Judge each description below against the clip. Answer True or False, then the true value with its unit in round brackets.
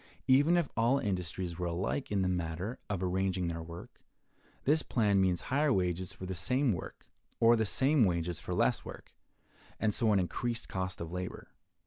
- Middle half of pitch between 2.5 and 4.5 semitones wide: False (4.9 semitones)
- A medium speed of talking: True (180 wpm)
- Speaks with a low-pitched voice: True (95 Hz)